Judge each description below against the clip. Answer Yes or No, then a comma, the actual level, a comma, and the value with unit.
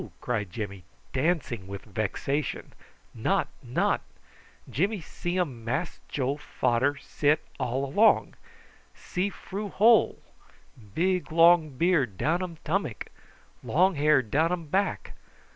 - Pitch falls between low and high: Yes, medium, 150 Hz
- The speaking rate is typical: No, slow, 115 wpm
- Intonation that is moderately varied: No, wide, 6.3 semitones